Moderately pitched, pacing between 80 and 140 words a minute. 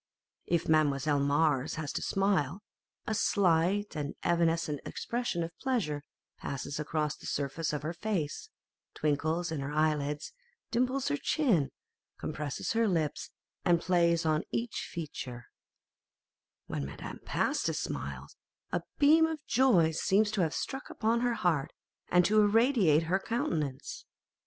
Yes: medium, 165 Hz; slow, 135 wpm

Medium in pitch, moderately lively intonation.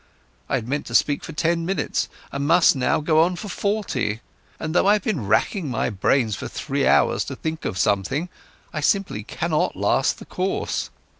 No: medium, 155 Hz; wide, 6.7 semitones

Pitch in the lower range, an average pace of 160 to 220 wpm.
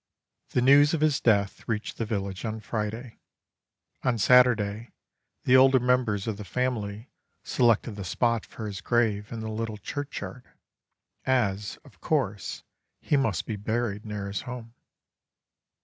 No: low, 115 Hz; average, 145 wpm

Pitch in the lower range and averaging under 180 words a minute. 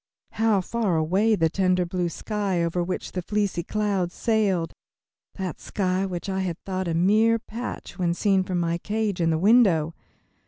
No: medium, 185 Hz; average, 170 wpm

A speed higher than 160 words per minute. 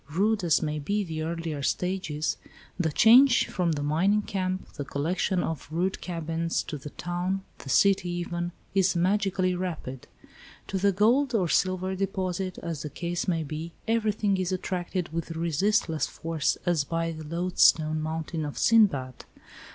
No: average, 155 wpm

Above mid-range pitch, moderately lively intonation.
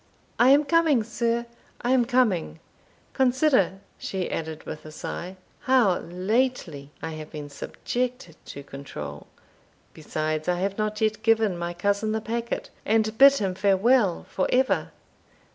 No: high, 210 Hz; wide, 6.1 semitones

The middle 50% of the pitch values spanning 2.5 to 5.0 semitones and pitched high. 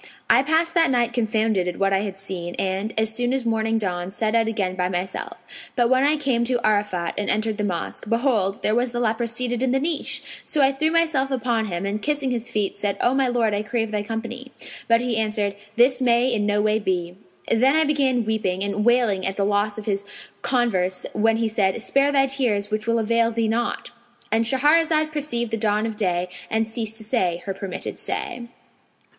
Yes: average, 3.4 semitones; high, 225 Hz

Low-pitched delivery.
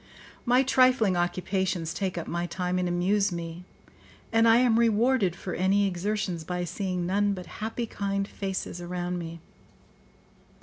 No: high, 190 Hz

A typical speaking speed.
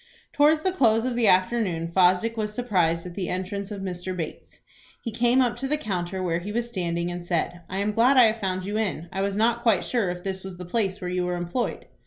No: fast, 245 wpm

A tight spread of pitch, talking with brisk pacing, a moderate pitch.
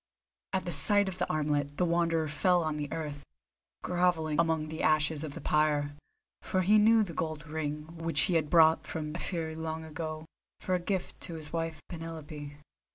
No: narrow, 2.1 semitones; average, 185 wpm; medium, 160 Hz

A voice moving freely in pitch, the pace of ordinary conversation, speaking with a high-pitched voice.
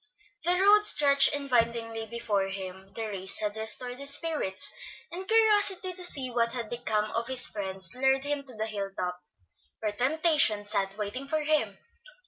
Yes: wide, 5.9 semitones; average, 165 wpm; high, 235 Hz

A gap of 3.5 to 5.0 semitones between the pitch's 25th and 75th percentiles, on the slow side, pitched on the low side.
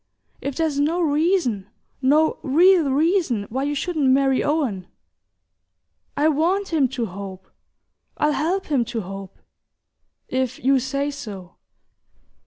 No: average, 4.6 semitones; slow, 125 wpm; very high, 280 Hz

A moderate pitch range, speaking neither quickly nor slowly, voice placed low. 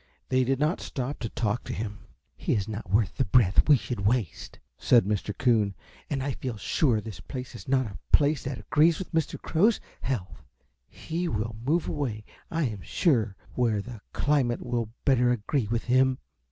Yes: average, 4.5 semitones; average, 185 wpm; low, 125 Hz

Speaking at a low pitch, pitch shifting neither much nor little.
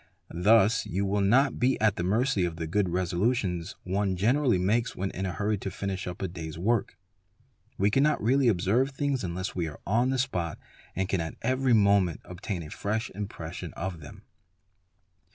Yes: low, 100 Hz; average, 4.5 semitones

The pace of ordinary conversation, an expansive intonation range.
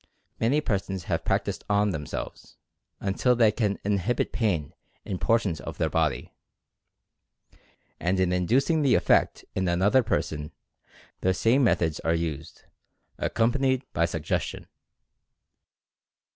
No: slow, 120 wpm; wide, 5.8 semitones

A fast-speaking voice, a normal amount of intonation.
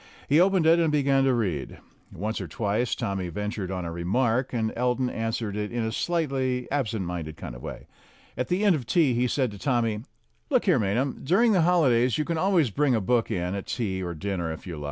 No: fast, 220 wpm; wide, 6.2 semitones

